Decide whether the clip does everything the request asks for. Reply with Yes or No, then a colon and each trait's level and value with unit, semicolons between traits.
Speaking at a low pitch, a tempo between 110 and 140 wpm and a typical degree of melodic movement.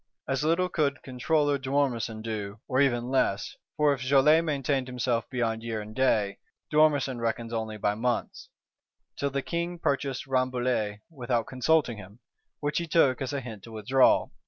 No: low, 130 Hz; average, 160 wpm; average, 3.7 semitones